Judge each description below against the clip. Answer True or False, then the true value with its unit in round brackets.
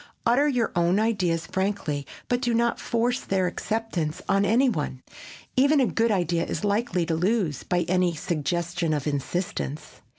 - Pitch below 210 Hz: True (185 Hz)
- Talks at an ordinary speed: True (160 wpm)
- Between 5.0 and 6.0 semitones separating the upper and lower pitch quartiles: True (5.4 semitones)